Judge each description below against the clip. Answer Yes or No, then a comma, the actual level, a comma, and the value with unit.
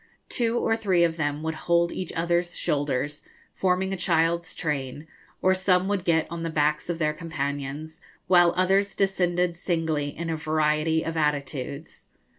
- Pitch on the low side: No, medium, 165 Hz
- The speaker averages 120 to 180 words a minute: Yes, average, 160 wpm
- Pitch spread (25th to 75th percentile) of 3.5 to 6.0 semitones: No, average, 2.8 semitones